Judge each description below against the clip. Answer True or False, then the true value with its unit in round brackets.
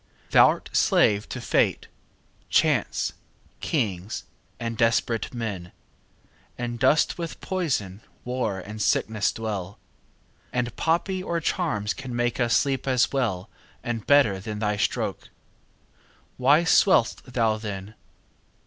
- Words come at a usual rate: False (120 wpm)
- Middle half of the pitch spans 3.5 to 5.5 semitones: True (4.3 semitones)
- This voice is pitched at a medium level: False (115 Hz)